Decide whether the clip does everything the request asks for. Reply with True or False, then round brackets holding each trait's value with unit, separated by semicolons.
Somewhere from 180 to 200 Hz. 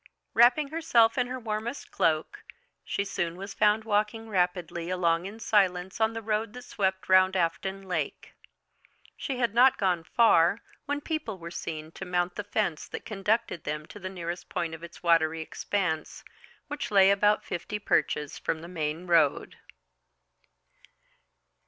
True (190 Hz)